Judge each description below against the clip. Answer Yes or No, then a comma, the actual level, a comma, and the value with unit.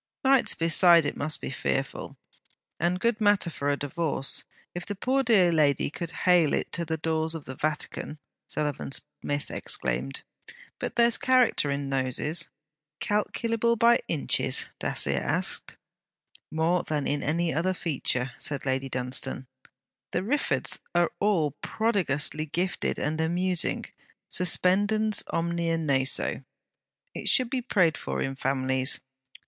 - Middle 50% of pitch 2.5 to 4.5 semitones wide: No, average, 5.2 semitones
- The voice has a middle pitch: Yes, medium, 165 Hz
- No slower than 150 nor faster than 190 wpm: No, slow, 135 wpm